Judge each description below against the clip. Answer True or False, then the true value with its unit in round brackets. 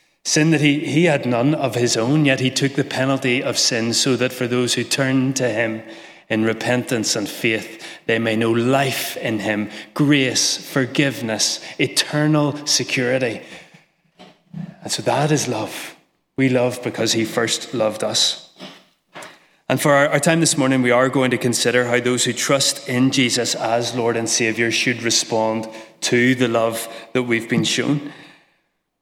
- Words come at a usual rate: True (165 wpm)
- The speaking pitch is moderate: False (125 Hz)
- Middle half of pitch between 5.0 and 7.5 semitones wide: False (3.3 semitones)